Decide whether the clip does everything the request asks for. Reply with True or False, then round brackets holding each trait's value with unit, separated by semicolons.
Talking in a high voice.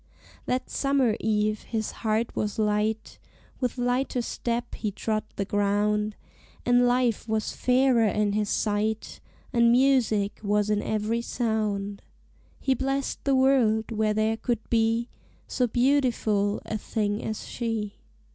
True (220 Hz)